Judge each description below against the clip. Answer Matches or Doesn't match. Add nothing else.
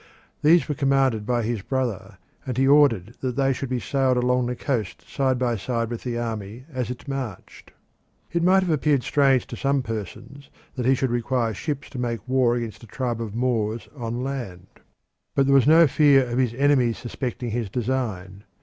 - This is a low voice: Matches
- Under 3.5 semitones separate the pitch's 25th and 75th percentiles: Matches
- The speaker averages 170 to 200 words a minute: Matches